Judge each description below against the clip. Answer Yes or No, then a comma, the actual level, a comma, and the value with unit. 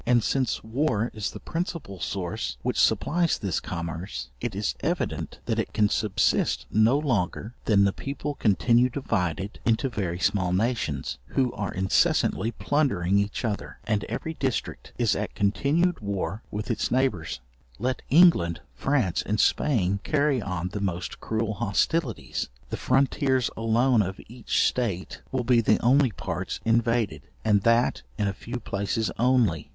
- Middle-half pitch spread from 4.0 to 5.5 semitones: Yes, average, 4.7 semitones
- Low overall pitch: Yes, low, 110 Hz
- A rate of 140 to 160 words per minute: Yes, average, 150 wpm